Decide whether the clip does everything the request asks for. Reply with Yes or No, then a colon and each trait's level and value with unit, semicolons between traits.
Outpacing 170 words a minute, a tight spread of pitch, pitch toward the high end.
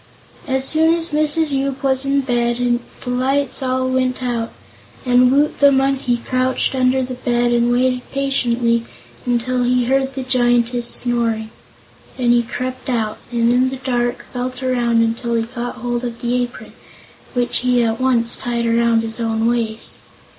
No: average, 165 wpm; narrow, 1.6 semitones; high, 245 Hz